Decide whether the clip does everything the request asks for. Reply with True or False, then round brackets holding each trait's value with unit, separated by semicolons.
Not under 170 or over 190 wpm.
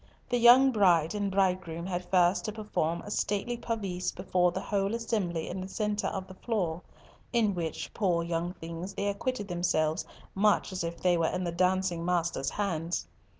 True (180 wpm)